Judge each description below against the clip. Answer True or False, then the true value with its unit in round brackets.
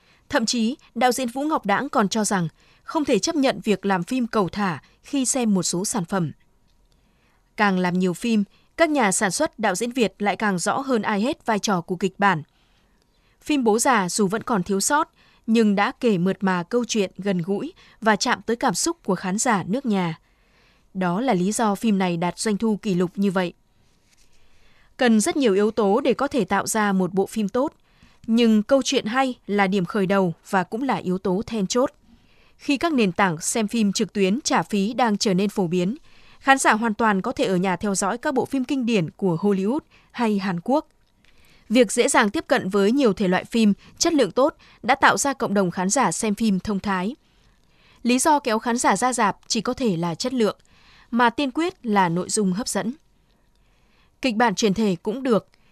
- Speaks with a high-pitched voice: True (215 Hz)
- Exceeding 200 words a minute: True (220 wpm)